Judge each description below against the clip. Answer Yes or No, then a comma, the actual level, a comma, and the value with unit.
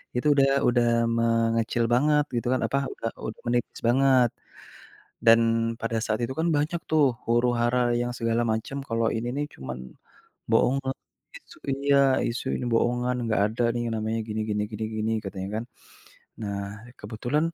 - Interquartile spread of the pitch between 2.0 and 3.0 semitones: Yes, narrow, 2.5 semitones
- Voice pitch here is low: Yes, low, 120 Hz